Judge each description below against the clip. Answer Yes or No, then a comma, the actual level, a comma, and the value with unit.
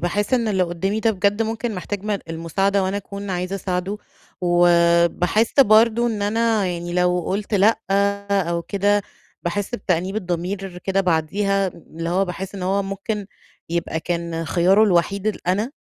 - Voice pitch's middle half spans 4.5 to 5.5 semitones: No, average, 2.7 semitones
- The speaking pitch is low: No, high, 195 Hz